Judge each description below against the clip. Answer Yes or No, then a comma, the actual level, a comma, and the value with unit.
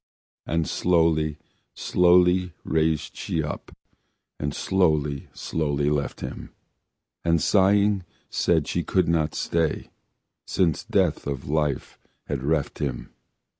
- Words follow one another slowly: Yes, slow, 110 wpm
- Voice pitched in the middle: No, very low, 80 Hz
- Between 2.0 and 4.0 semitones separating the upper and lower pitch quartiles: Yes, average, 3.1 semitones